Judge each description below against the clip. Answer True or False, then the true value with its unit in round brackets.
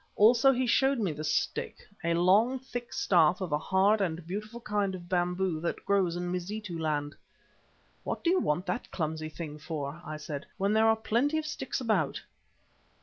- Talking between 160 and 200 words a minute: True (185 wpm)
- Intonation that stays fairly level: False (5.3 semitones)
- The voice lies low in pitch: False (185 Hz)